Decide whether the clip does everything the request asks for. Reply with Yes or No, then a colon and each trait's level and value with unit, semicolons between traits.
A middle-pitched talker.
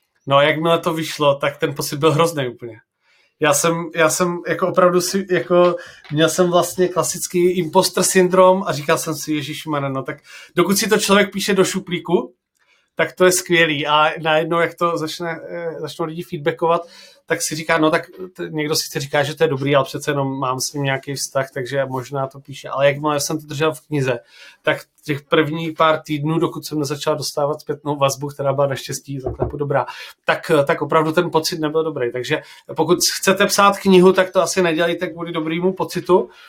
Yes: medium, 160 Hz